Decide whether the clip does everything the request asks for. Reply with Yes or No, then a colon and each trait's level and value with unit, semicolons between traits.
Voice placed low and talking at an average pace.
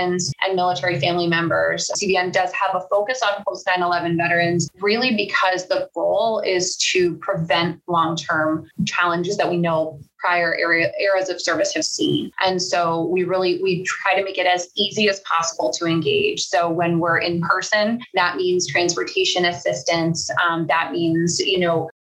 No: medium, 180 Hz; average, 165 wpm